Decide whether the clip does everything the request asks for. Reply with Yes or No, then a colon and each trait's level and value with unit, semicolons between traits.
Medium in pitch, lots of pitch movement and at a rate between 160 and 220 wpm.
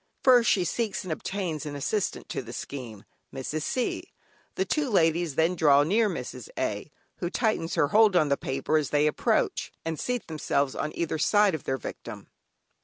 Yes: medium, 160 Hz; wide, 6.2 semitones; average, 180 wpm